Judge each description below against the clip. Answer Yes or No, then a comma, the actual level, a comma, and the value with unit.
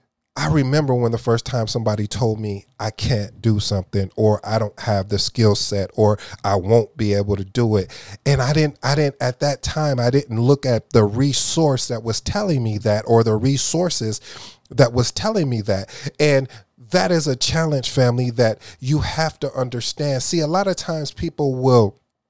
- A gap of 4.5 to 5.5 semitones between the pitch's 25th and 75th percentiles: Yes, average, 4.8 semitones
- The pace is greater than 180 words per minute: Yes, average, 195 wpm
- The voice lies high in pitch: No, low, 120 Hz